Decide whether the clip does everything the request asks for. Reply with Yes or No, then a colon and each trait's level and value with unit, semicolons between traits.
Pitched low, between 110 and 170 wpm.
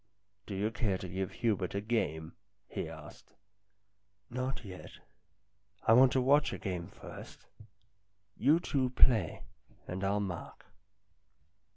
Yes: low, 100 Hz; average, 140 wpm